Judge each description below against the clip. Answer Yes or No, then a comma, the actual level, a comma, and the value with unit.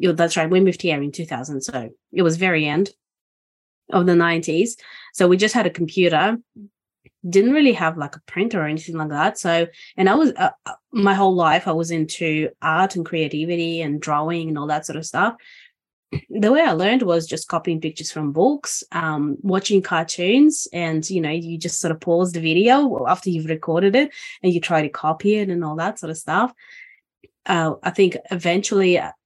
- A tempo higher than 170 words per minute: Yes, average, 195 wpm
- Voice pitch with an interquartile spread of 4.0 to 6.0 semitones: No, average, 3.6 semitones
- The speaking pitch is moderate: Yes, medium, 170 Hz